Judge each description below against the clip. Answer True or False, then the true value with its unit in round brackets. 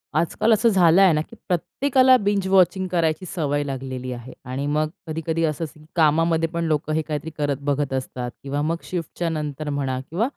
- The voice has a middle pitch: True (155 Hz)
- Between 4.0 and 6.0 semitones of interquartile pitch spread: False (3.5 semitones)